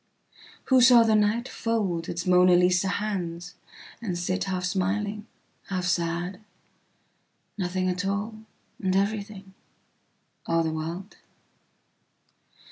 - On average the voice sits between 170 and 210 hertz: Yes, high, 190 Hz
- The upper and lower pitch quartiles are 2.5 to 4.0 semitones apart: Yes, average, 2.9 semitones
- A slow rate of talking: Yes, slow, 85 wpm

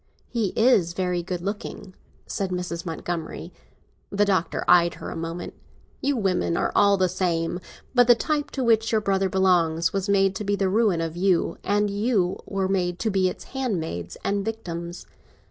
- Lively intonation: No, average, 3.0 semitones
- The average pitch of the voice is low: No, high, 190 Hz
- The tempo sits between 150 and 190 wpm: Yes, average, 180 wpm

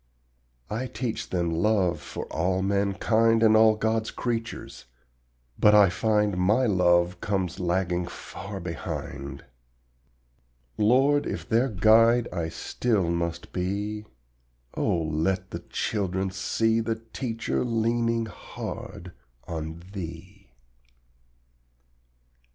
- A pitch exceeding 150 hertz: No, low, 100 Hz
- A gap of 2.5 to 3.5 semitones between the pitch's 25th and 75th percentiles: No, average, 4.2 semitones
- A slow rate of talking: Yes, slow, 105 wpm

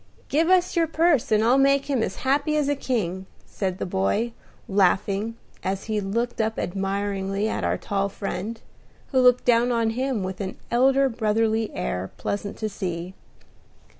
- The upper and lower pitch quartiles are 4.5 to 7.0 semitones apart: Yes, average, 4.9 semitones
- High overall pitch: Yes, high, 220 Hz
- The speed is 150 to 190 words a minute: Yes, average, 165 wpm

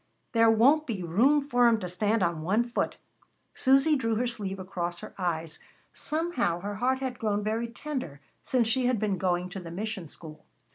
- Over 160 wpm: Yes, average, 190 wpm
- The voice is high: Yes, high, 220 Hz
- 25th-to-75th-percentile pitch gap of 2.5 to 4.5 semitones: No, wide, 5.5 semitones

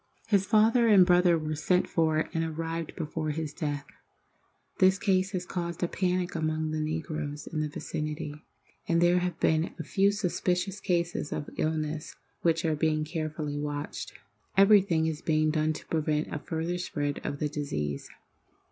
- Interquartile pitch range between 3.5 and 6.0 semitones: No, average, 2.7 semitones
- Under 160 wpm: No, average, 165 wpm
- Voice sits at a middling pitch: Yes, medium, 160 Hz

